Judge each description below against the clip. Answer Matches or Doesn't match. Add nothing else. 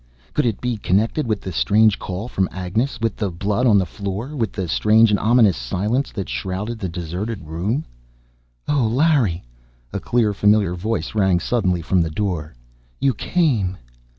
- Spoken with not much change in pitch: Doesn't match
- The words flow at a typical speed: Matches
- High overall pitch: Doesn't match